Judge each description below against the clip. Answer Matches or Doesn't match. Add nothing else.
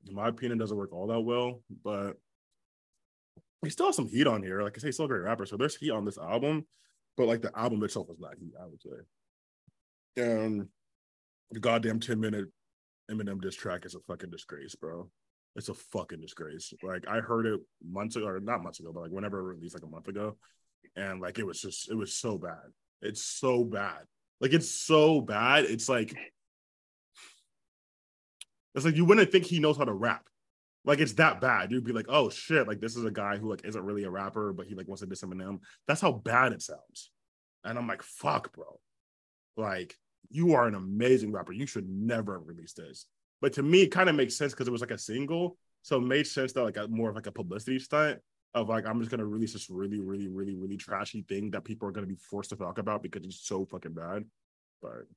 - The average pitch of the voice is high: Doesn't match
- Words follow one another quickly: Matches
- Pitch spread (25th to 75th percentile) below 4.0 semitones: Doesn't match